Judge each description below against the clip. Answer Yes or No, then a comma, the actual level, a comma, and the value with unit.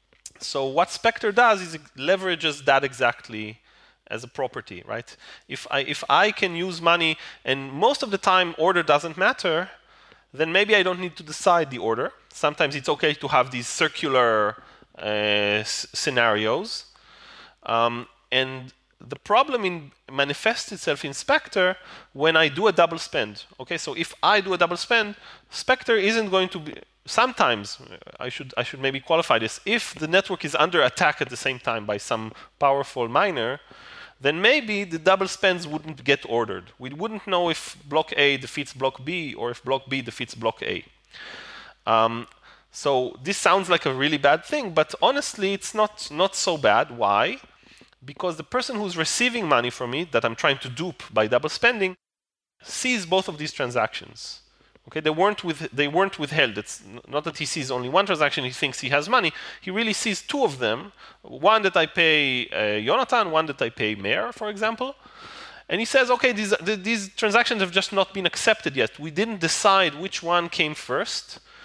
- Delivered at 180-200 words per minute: Yes, average, 185 wpm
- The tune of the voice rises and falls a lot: Yes, wide, 6.5 semitones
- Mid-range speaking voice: Yes, medium, 165 Hz